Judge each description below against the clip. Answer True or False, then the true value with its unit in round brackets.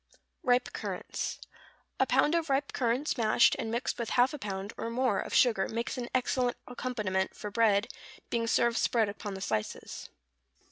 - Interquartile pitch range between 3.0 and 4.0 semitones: True (3.3 semitones)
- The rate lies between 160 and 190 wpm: True (170 wpm)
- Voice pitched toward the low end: False (235 Hz)